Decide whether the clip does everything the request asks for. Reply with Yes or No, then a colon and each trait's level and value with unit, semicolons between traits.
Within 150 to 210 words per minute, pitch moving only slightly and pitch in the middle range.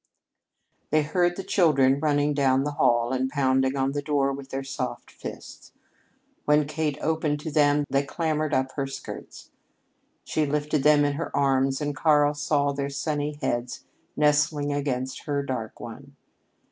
Yes: average, 160 wpm; narrow, 1.8 semitones; medium, 145 Hz